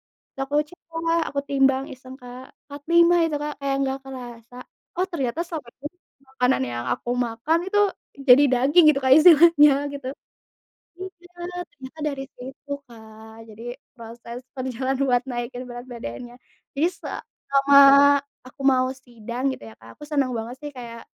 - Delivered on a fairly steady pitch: No, average, 3.1 semitones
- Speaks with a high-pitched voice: Yes, very high, 265 Hz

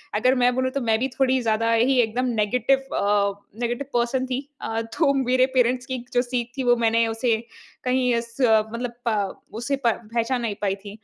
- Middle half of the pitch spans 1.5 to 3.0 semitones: Yes, narrow, 2.4 semitones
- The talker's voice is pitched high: Yes, high, 240 Hz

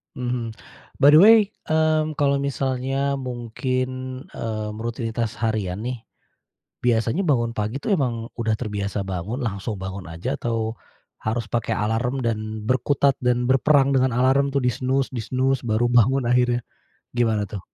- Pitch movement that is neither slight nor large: Yes, average, 3.1 semitones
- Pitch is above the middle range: No, low, 120 Hz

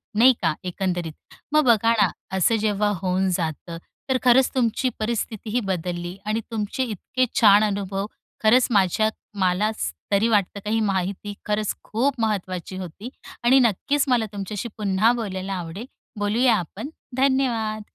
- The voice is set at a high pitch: Yes, high, 210 Hz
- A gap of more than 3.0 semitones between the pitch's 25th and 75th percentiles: Yes, average, 3.5 semitones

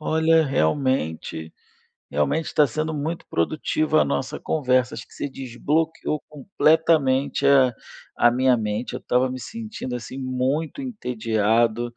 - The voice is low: Yes, low, 130 Hz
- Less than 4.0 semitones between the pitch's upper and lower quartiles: No, average, 4.3 semitones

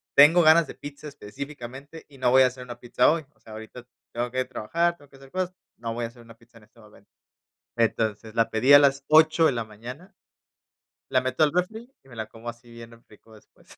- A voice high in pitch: No, low, 125 Hz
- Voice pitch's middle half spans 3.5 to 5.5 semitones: Yes, average, 4.1 semitones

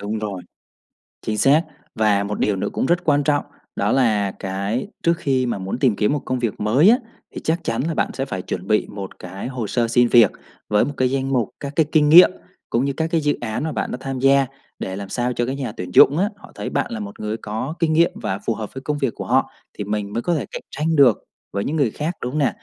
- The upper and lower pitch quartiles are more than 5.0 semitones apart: Yes, wide, 5.5 semitones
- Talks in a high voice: No, low, 125 Hz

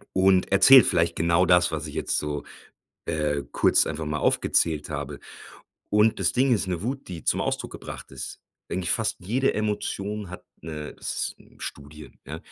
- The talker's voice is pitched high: No, very low, 90 Hz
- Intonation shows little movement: No, wide, 5.5 semitones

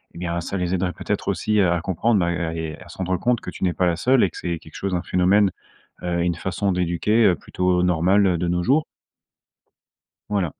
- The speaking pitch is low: Yes, very low, 90 Hz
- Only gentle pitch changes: Yes, narrow, 2.2 semitones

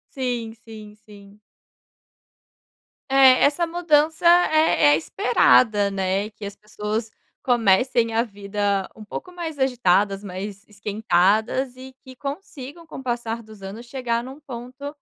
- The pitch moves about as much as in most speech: Yes, average, 4.7 semitones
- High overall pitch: Yes, high, 230 Hz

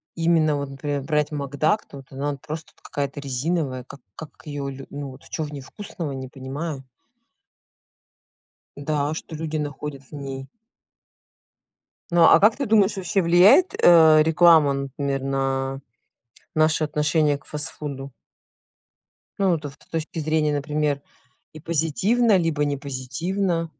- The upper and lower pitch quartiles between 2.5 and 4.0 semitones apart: Yes, average, 2.8 semitones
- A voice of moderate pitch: Yes, medium, 150 Hz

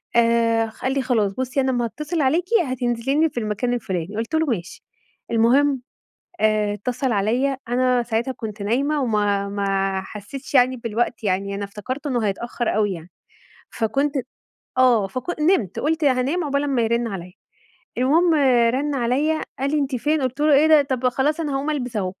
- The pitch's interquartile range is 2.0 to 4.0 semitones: No, average, 4.4 semitones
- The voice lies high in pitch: Yes, high, 245 Hz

